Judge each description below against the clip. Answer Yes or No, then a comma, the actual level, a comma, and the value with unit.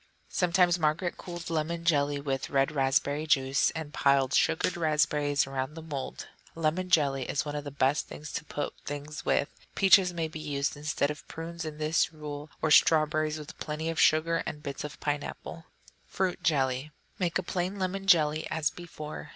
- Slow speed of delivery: No, average, 175 wpm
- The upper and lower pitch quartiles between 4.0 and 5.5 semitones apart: No, narrow, 2.4 semitones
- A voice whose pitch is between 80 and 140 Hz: No, medium, 155 Hz